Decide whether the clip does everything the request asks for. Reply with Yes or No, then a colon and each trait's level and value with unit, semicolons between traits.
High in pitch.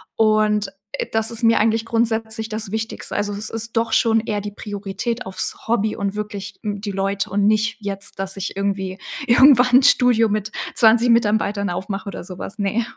Yes: high, 215 Hz